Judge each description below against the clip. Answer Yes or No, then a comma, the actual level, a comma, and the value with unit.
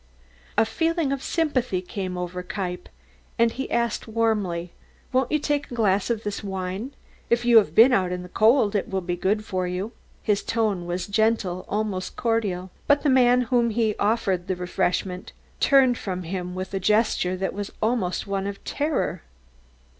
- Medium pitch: No, high, 205 Hz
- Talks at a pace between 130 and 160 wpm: No, average, 180 wpm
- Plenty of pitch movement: No, average, 4.3 semitones